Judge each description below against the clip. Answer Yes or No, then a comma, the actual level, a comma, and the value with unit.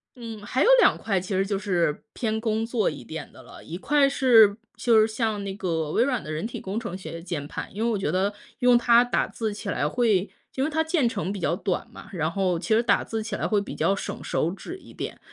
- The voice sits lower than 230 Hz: Yes, high, 215 Hz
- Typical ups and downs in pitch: Yes, average, 4.0 semitones